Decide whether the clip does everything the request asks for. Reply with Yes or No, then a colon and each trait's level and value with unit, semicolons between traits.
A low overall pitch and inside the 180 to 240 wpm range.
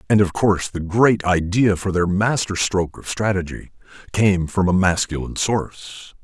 No: very low, 95 Hz; average, 165 wpm